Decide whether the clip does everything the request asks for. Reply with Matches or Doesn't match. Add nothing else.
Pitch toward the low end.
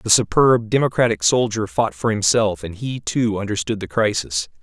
Matches